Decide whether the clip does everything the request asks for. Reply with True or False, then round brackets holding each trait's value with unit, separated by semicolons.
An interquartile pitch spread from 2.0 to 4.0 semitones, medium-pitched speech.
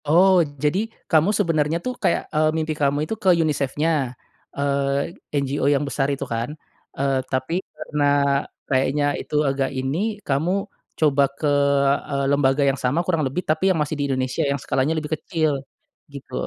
True (2.4 semitones; 145 Hz)